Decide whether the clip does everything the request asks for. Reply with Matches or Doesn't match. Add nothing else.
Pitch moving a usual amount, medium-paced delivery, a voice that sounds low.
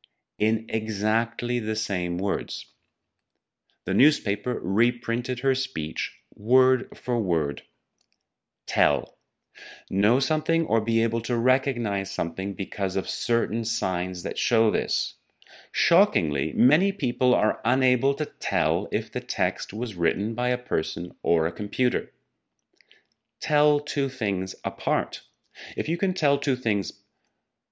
Doesn't match